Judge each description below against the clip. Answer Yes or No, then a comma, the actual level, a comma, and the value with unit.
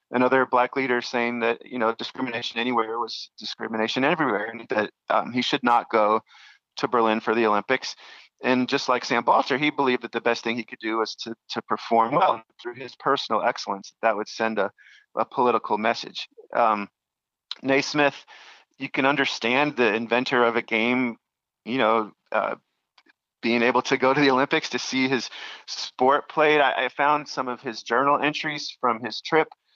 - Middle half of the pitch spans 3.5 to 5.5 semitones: No, average, 2.9 semitones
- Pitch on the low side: Yes, low, 125 Hz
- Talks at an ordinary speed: Yes, average, 185 wpm